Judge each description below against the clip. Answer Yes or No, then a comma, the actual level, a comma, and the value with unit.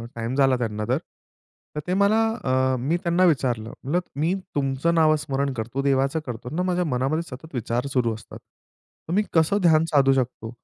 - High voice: No, low, 135 Hz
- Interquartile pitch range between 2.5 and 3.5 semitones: No, average, 4.4 semitones